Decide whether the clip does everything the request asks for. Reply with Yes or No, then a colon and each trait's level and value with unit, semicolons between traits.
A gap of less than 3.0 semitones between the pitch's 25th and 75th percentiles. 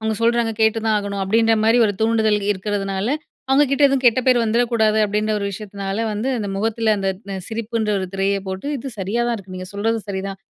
Yes: narrow, 2.5 semitones